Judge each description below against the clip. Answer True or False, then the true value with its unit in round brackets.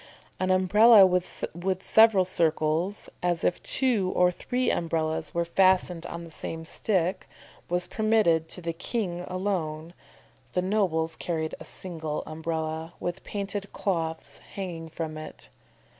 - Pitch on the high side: False (175 Hz)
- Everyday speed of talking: False (130 wpm)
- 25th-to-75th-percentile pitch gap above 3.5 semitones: False (2.8 semitones)